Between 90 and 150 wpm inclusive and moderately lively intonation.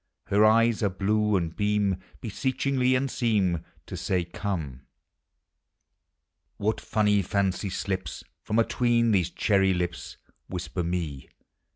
Yes: average, 140 wpm; average, 3.3 semitones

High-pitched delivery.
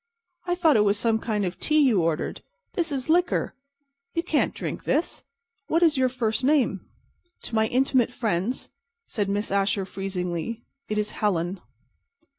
Yes: high, 220 Hz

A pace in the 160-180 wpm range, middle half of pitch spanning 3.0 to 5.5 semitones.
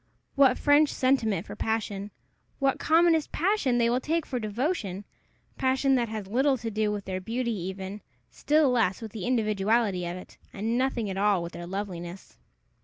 Yes: average, 175 wpm; average, 5.1 semitones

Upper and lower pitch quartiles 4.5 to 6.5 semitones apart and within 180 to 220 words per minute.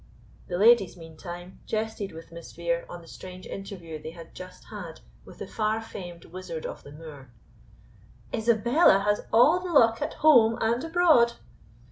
No: average, 5.2 semitones; average, 160 wpm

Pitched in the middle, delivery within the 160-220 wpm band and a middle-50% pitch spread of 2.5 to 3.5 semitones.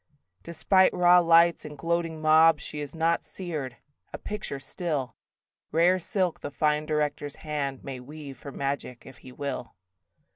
No: medium, 150 Hz; average, 150 wpm; average, 3.2 semitones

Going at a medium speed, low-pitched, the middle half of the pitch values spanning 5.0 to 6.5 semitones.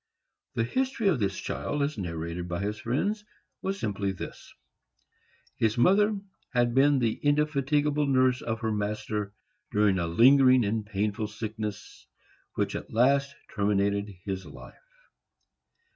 No: slow, 130 wpm; low, 110 Hz; wide, 5.5 semitones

